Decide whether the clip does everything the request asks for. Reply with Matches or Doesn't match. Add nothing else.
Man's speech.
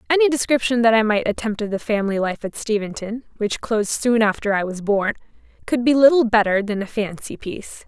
Doesn't match